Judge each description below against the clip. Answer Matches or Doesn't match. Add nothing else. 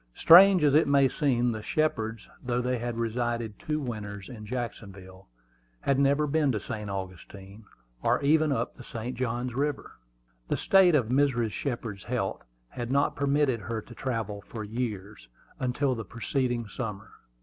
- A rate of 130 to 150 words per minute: Doesn't match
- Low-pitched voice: Matches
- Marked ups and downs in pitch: Doesn't match